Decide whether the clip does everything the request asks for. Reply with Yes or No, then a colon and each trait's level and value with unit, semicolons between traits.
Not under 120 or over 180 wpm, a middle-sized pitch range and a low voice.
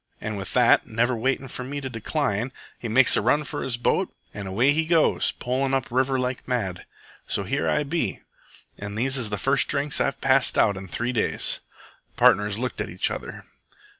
No: average, 200 wpm; average, 3.9 semitones; low, 125 Hz